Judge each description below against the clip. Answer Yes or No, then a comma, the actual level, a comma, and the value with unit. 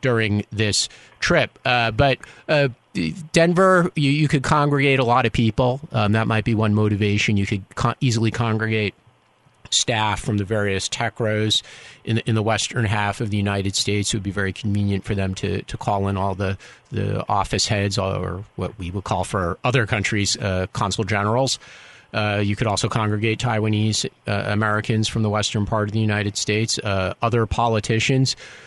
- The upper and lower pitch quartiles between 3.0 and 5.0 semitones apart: No, narrow, 2.6 semitones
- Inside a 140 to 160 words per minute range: No, average, 185 wpm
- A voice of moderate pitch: No, low, 110 Hz